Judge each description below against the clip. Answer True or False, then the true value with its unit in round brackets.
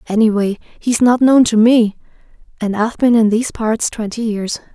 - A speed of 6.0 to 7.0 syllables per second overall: False (5.0 syllables/s)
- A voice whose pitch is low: False (225 Hz)